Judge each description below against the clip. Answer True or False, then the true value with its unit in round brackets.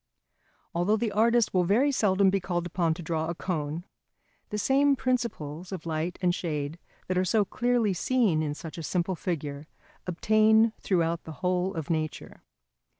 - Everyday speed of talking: True (165 wpm)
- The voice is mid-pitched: True (180 Hz)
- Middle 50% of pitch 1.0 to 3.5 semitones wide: False (4.8 semitones)